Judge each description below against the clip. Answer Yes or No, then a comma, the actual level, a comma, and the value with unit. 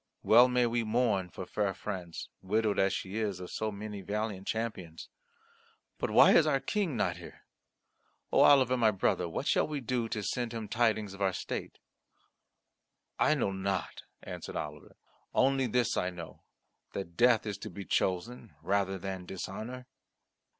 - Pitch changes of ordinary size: Yes, average, 3.9 semitones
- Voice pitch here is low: Yes, low, 105 Hz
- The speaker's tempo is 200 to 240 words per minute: No, average, 165 wpm